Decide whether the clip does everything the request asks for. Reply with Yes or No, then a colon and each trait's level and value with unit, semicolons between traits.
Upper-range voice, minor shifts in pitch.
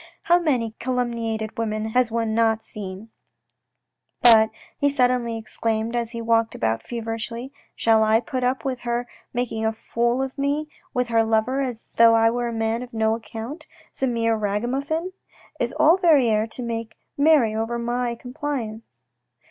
Yes: high, 230 Hz; narrow, 2.1 semitones